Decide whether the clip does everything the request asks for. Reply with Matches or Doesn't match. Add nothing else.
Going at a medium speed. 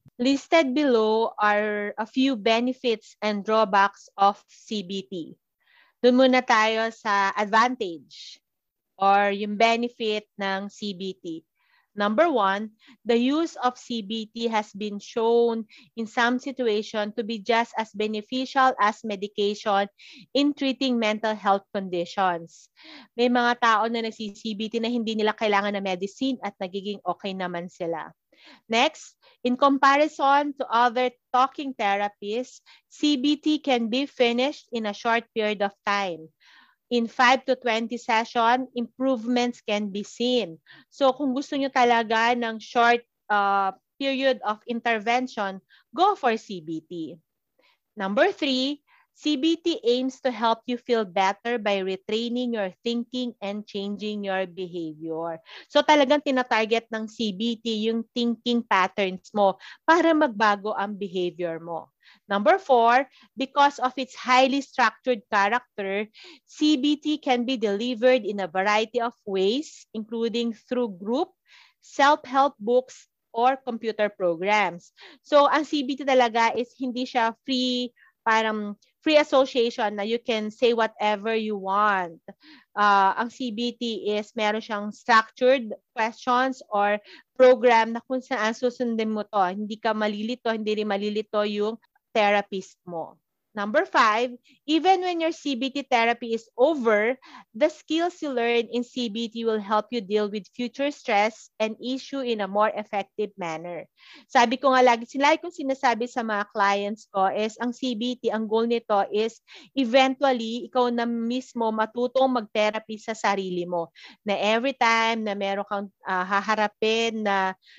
Matches